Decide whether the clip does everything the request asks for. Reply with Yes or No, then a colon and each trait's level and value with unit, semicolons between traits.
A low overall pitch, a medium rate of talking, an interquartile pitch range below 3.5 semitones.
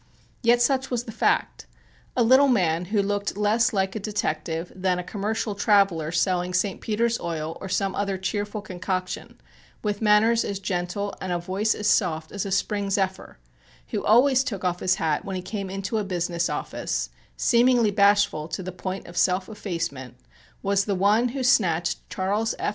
No: high, 195 Hz; average, 180 wpm; average, 2.8 semitones